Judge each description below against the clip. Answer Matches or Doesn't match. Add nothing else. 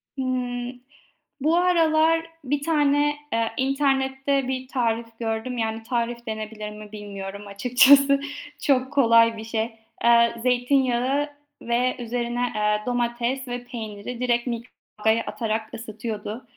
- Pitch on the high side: Matches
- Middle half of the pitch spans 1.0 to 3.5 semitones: Matches